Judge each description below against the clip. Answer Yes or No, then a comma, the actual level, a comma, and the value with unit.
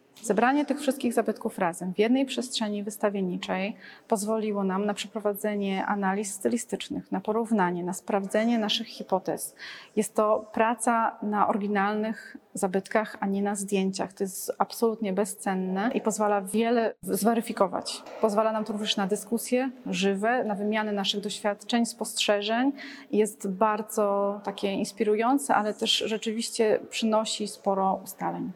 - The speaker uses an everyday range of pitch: No, narrow, 2.1 semitones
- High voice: Yes, high, 215 Hz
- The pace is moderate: Yes, average, 130 wpm